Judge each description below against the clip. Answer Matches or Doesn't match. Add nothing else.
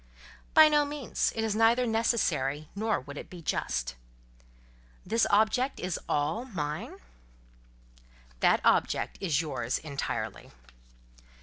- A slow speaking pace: Matches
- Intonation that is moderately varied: Doesn't match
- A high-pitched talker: Matches